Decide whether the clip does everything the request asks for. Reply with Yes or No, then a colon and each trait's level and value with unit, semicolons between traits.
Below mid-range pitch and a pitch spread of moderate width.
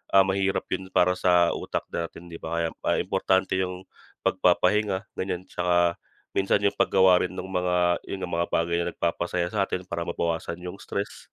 No: very low, 90 Hz; narrow, 1.6 semitones